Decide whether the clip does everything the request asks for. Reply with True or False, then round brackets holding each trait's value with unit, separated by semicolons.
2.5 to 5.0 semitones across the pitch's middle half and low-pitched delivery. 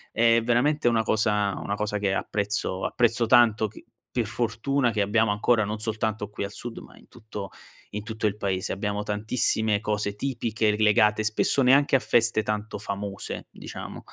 False (2.0 semitones; 110 Hz)